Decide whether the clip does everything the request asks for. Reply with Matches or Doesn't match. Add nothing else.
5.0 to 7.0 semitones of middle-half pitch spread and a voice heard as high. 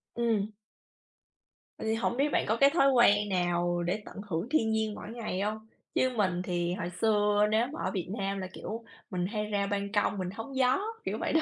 Doesn't match